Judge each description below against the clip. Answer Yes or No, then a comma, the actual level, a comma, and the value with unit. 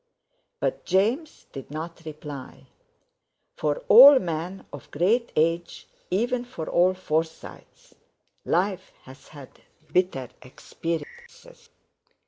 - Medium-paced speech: No, slow, 100 wpm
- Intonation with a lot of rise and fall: Yes, wide, 6.9 semitones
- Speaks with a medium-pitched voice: Yes, medium, 175 Hz